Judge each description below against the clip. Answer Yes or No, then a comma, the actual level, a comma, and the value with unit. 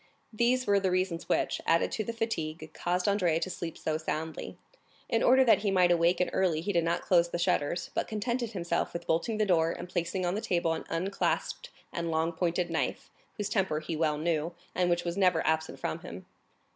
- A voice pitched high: No, medium, 175 Hz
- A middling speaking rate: No, fast, 210 wpm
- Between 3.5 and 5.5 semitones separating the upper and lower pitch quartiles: No, average, 2.9 semitones